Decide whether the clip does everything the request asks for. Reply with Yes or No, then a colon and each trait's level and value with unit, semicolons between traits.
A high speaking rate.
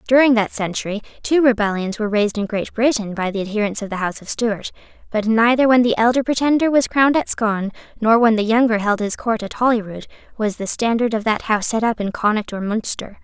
Yes: fast, 220 wpm